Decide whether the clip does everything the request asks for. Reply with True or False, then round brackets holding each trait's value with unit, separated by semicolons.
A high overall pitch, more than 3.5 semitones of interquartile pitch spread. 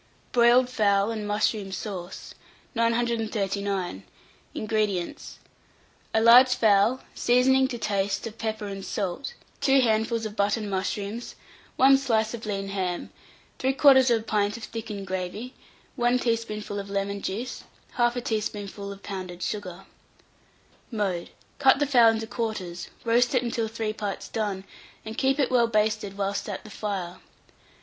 False (215 Hz; 3.0 semitones)